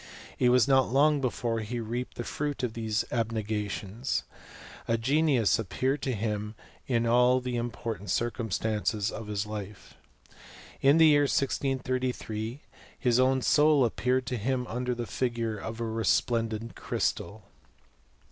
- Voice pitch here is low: Yes, low, 120 Hz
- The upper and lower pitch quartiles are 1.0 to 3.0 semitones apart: Yes, average, 2.7 semitones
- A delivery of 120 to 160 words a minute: Yes, average, 150 wpm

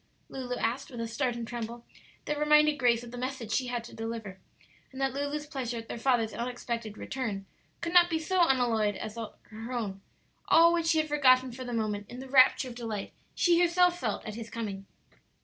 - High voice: Yes, high, 245 Hz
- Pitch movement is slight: No, average, 3.9 semitones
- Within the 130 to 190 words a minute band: No, fast, 205 wpm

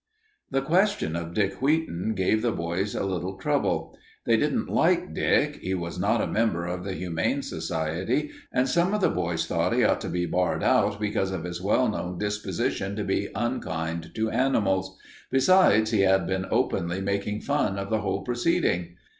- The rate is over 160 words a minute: Yes, average, 180 wpm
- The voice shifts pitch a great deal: No, average, 4.0 semitones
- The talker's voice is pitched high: No, very low, 95 Hz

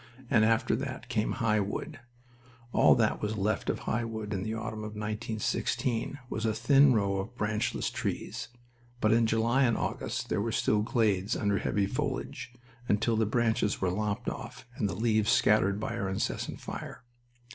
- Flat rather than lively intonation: Yes, narrow, 1.7 semitones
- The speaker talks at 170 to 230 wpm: Yes, average, 175 wpm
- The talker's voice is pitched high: No, low, 110 Hz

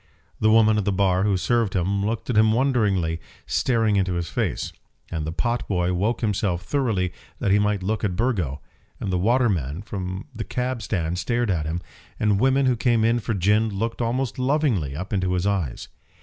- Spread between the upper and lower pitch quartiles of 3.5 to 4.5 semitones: Yes, average, 4.1 semitones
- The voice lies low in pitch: Yes, low, 105 Hz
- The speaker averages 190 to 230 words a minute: Yes, average, 195 wpm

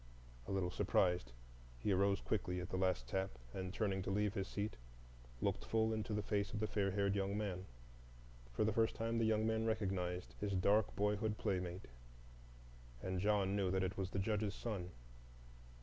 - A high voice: No, low, 100 Hz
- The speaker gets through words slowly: No, average, 180 wpm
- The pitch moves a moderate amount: No, narrow, 2.3 semitones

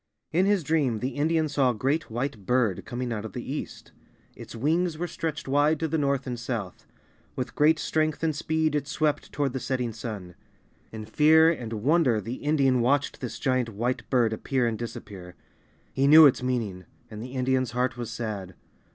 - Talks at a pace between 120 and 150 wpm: No, average, 190 wpm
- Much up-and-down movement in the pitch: No, average, 4.5 semitones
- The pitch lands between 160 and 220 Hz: No, low, 130 Hz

